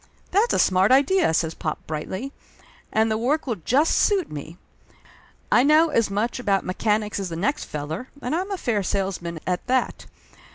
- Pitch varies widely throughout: Yes, wide, 7.2 semitones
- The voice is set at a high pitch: Yes, high, 220 Hz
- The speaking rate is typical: Yes, average, 175 wpm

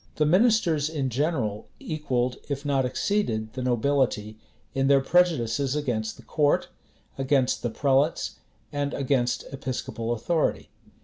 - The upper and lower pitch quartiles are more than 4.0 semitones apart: No, average, 3.6 semitones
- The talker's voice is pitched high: No, low, 135 Hz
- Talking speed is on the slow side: Yes, slow, 125 wpm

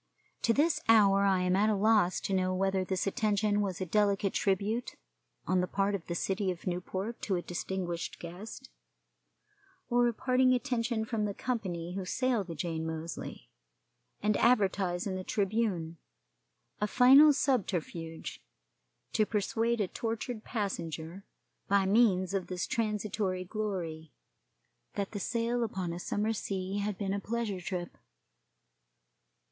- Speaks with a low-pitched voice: No, high, 200 Hz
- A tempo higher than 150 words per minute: No, average, 145 wpm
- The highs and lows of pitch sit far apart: No, average, 3.3 semitones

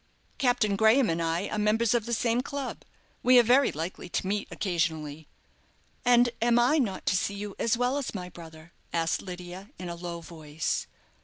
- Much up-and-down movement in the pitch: Yes, wide, 5.9 semitones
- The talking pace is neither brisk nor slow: Yes, average, 185 wpm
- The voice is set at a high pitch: Yes, high, 200 Hz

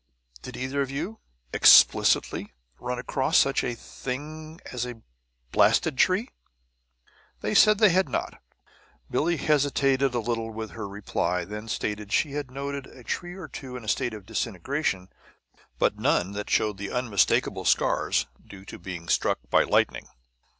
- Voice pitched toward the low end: Yes, low, 125 Hz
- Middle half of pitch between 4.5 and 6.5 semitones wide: Yes, average, 5.2 semitones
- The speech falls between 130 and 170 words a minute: Yes, average, 155 wpm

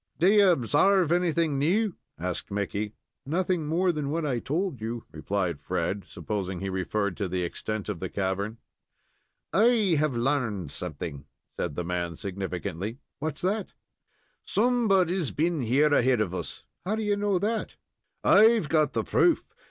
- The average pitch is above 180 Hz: No, low, 135 Hz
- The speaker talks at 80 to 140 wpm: No, average, 150 wpm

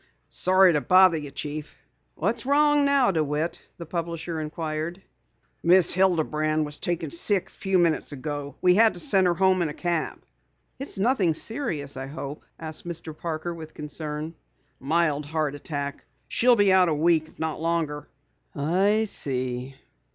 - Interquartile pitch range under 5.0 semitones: Yes, average, 3.7 semitones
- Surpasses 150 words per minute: Yes, average, 160 wpm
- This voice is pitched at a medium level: Yes, medium, 165 Hz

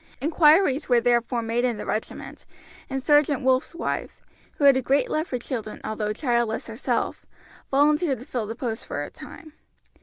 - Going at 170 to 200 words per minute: Yes, average, 175 wpm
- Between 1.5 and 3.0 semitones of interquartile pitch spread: No, average, 3.9 semitones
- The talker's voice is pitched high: Yes, very high, 255 Hz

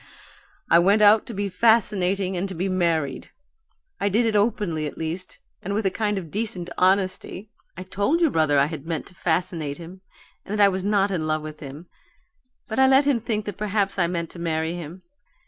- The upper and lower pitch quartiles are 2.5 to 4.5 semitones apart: Yes, average, 3.7 semitones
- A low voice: No, medium, 185 Hz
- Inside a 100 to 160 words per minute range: No, fast, 205 wpm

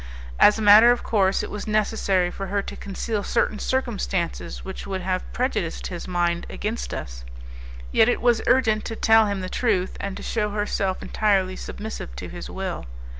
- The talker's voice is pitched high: Yes, high, 205 Hz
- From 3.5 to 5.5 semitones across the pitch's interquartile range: No, average, 2.9 semitones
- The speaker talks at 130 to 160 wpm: No, average, 180 wpm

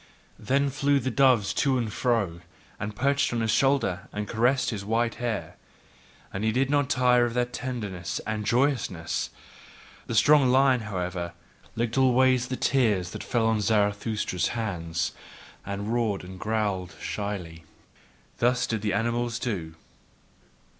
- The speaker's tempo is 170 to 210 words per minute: No, average, 140 wpm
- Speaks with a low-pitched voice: Yes, low, 115 Hz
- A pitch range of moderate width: Yes, average, 3.8 semitones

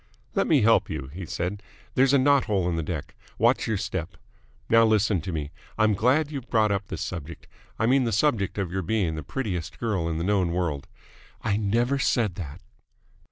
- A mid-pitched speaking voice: No, low, 100 Hz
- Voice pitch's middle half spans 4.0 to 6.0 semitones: Yes, average, 5.1 semitones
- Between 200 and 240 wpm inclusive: Yes, fast, 205 wpm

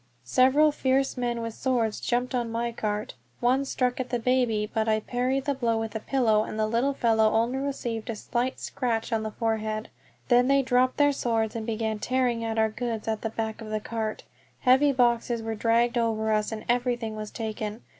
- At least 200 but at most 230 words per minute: Yes, fast, 205 wpm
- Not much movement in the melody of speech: Yes, narrow, 2.3 semitones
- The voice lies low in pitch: No, high, 230 Hz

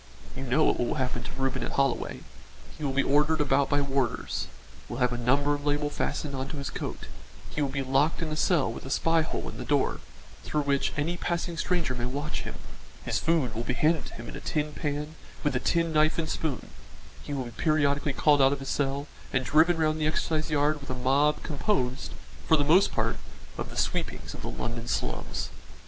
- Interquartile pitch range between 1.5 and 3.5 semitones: Yes, narrow, 2.6 semitones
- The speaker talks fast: Yes, fast, 225 wpm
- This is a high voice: No, medium, 145 Hz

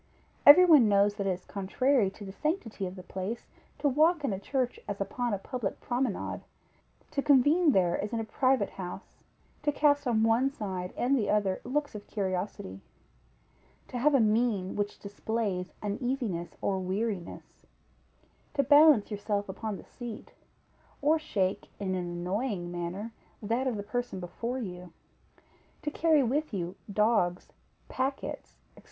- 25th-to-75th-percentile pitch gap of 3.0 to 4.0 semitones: No, wide, 5.4 semitones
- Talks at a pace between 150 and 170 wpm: Yes, average, 160 wpm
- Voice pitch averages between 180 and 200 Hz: No, high, 215 Hz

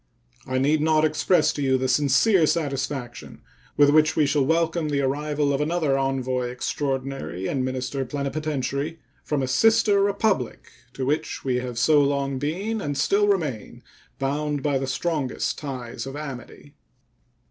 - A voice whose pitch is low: No, medium, 145 Hz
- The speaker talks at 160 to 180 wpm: No, average, 150 wpm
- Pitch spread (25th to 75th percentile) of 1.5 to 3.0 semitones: Yes, narrow, 2.6 semitones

